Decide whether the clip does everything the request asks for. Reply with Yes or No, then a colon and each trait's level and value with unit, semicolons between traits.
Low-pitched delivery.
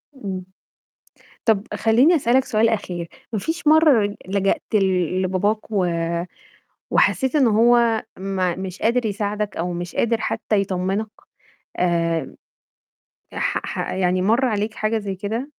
No: high, 210 Hz